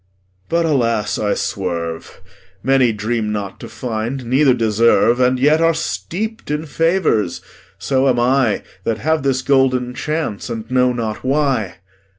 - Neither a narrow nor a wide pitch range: Yes, average, 4.0 semitones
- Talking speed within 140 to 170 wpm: Yes, average, 145 wpm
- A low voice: Yes, low, 125 Hz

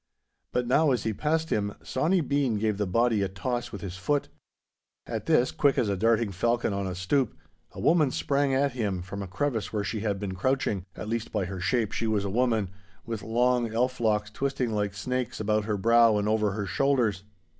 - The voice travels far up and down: No, average, 3.9 semitones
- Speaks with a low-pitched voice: Yes, low, 110 Hz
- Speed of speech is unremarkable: No, fast, 210 wpm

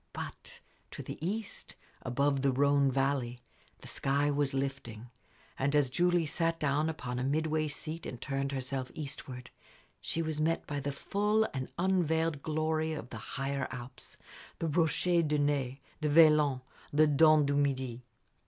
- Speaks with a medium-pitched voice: Yes, medium, 145 Hz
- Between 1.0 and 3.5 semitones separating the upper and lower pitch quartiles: Yes, average, 2.8 semitones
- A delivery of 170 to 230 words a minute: No, average, 155 wpm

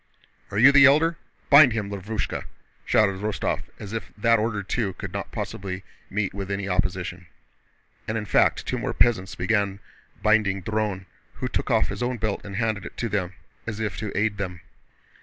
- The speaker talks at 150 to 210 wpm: Yes, average, 180 wpm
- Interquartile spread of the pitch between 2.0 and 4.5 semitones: Yes, narrow, 2.4 semitones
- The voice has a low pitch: Yes, low, 105 Hz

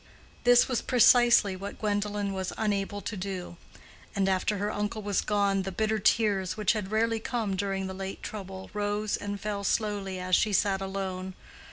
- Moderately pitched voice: No, high, 200 Hz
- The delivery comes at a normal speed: Yes, average, 175 wpm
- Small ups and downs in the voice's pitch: Yes, narrow, 1.8 semitones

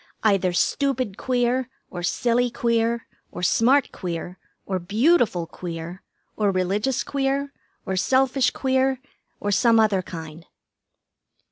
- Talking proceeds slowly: Yes, slow, 115 wpm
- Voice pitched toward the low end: No, high, 225 Hz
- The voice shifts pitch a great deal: Yes, wide, 5.9 semitones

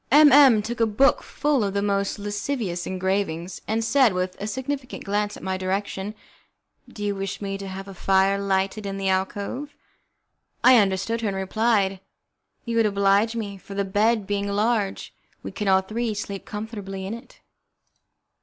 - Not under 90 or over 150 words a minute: No, average, 180 wpm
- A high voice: Yes, high, 205 Hz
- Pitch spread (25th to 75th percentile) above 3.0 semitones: No, narrow, 2.6 semitones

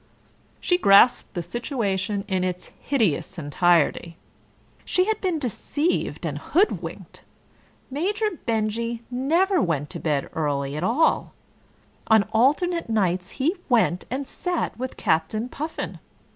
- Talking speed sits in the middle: No, slow, 120 wpm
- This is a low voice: No, high, 225 Hz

